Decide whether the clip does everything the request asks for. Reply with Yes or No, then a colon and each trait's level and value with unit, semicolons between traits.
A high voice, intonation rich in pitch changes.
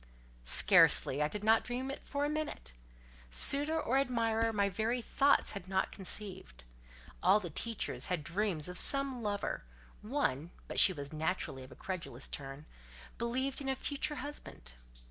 Yes: high, 210 Hz; wide, 8.3 semitones